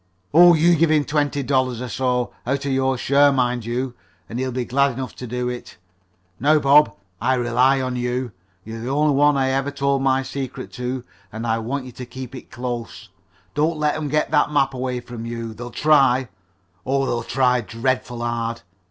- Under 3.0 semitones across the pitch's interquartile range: Yes, narrow, 2.4 semitones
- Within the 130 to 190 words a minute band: No, average, 200 wpm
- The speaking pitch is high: No, low, 130 Hz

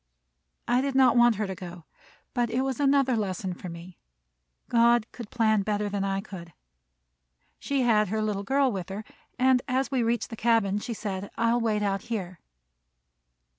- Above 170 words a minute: Yes, average, 180 wpm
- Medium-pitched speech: No, high, 220 Hz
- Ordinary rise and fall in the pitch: Yes, average, 3.7 semitones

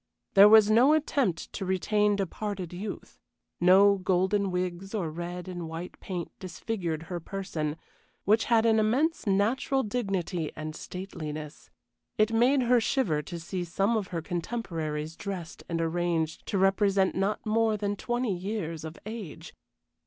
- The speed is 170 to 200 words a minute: No, average, 145 wpm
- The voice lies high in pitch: Yes, high, 195 Hz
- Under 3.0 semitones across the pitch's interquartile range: No, average, 3.9 semitones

